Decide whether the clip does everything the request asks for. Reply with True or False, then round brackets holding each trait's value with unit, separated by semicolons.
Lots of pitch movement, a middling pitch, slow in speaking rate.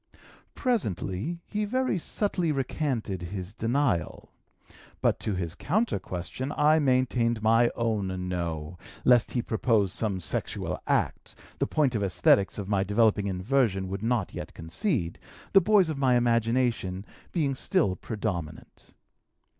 False (6.6 semitones; 115 Hz; 130 wpm)